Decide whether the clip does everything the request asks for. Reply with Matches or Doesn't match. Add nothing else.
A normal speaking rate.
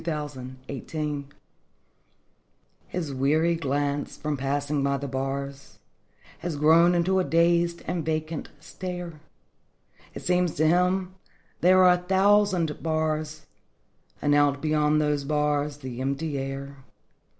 Doesn't match